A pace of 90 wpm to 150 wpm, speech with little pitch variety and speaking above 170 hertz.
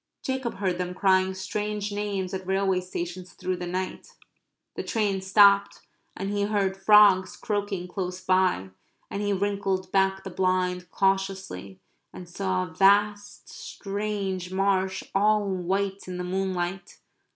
Yes: average, 140 wpm; narrow, 1.5 semitones; high, 190 Hz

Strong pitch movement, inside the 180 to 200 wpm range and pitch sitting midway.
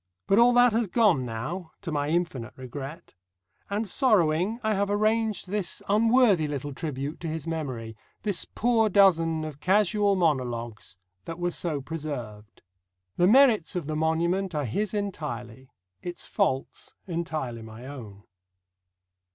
No: wide, 6.8 semitones; average, 140 wpm; medium, 165 Hz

